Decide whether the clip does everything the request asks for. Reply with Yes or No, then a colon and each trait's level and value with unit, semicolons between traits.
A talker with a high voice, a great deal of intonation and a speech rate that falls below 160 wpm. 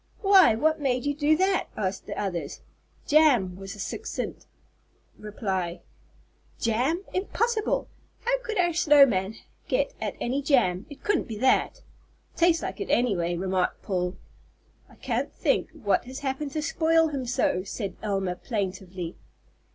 Yes: very high, 250 Hz; wide, 8.7 semitones; average, 150 wpm